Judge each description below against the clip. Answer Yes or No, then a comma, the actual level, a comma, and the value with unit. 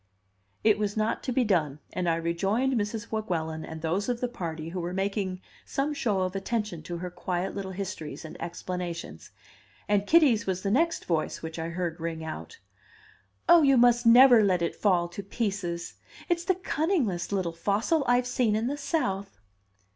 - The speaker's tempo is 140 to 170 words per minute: No, average, 185 wpm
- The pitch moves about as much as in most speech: No, wide, 5.7 semitones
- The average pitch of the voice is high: Yes, high, 195 Hz